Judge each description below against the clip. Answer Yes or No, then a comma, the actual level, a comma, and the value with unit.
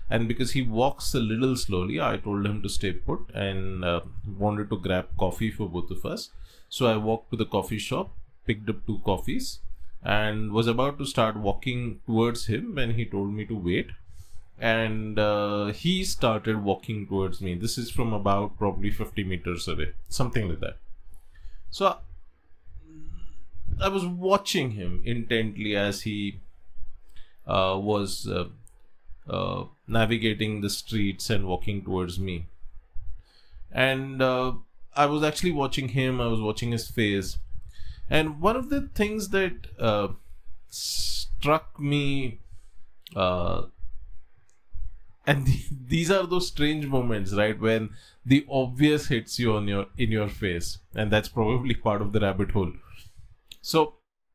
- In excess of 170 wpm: No, average, 150 wpm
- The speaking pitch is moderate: No, low, 105 Hz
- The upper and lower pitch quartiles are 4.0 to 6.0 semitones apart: Yes, average, 4.8 semitones